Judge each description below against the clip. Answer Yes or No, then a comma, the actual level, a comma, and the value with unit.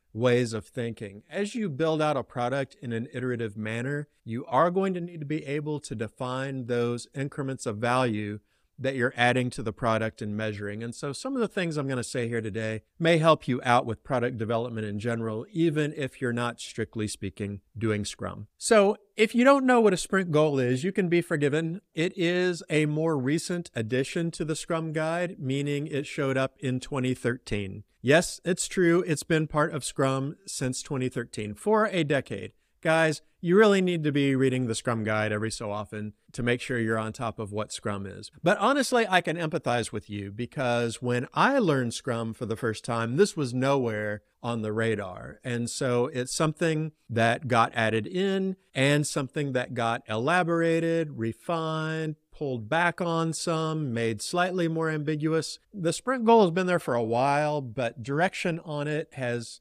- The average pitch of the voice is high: No, low, 135 Hz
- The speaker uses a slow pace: No, average, 190 wpm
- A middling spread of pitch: No, wide, 5.8 semitones